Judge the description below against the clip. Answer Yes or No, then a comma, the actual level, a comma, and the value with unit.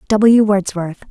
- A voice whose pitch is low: No, high, 200 Hz